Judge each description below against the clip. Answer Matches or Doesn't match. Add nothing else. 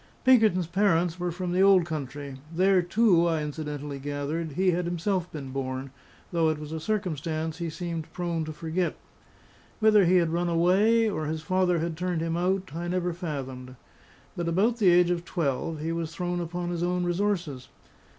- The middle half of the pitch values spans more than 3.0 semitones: Doesn't match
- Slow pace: Doesn't match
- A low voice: Doesn't match